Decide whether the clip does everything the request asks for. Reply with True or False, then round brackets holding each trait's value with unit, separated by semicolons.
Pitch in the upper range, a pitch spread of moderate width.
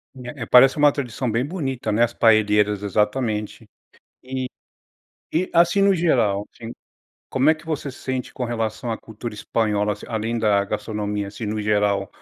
False (115 Hz; 3.9 semitones)